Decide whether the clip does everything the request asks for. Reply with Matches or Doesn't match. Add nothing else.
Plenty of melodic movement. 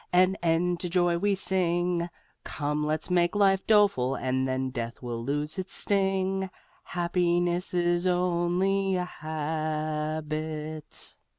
Doesn't match